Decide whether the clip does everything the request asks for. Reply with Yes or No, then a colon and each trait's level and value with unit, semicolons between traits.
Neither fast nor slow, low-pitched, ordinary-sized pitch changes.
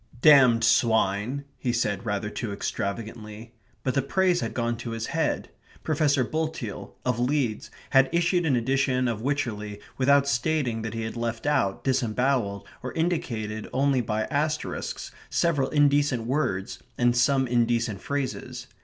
Yes: average, 145 wpm; low, 125 Hz; average, 4.1 semitones